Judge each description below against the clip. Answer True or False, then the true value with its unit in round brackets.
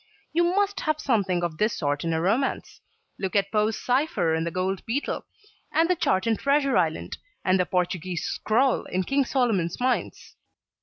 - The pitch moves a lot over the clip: True (7.3 semitones)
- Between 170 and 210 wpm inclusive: True (175 wpm)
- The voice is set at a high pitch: True (210 Hz)